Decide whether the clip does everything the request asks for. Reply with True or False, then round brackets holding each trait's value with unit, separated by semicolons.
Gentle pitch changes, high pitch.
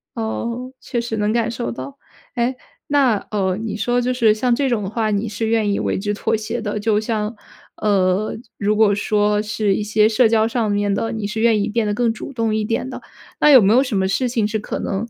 True (2.2 semitones; 220 Hz)